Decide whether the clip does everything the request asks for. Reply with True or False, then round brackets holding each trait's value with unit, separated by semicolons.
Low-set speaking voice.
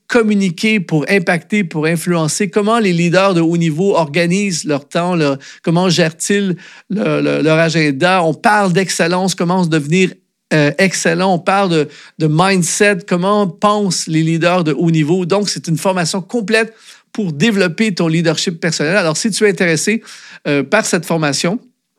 False (180 Hz)